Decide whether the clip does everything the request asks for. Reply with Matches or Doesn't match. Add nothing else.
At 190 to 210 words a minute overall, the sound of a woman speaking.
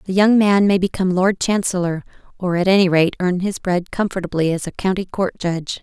Matches